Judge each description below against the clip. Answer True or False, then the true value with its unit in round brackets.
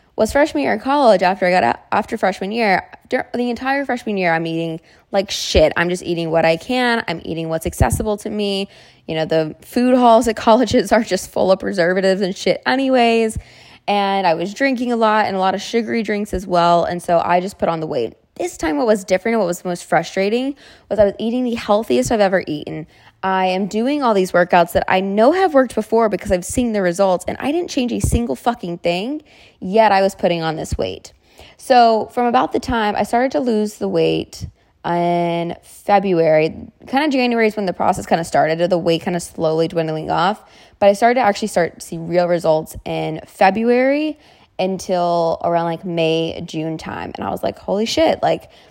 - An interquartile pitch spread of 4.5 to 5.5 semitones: True (5.1 semitones)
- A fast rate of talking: True (215 wpm)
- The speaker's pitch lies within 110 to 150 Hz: False (195 Hz)